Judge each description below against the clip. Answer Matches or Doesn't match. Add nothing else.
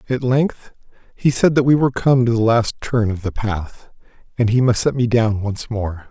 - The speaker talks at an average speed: Doesn't match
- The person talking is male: Matches